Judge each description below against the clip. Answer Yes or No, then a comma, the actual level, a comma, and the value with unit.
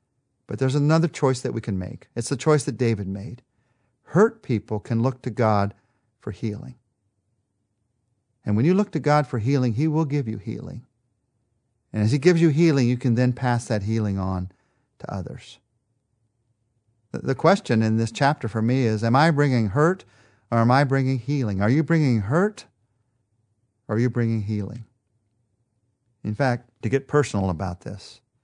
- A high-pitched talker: No, low, 120 Hz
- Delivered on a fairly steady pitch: No, average, 3.2 semitones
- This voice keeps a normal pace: Yes, average, 175 wpm